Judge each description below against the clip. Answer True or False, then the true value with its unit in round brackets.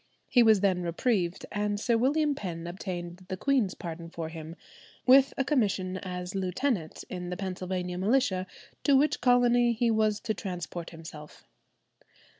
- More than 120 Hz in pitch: True (190 Hz)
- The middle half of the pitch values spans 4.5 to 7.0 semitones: True (5.2 semitones)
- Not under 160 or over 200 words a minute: False (150 wpm)